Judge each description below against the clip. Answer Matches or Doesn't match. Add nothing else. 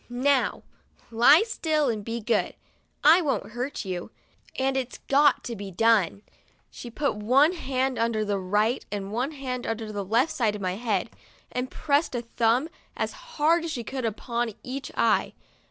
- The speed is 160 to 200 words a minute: Matches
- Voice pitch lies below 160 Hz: Doesn't match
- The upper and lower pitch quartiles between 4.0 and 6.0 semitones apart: Matches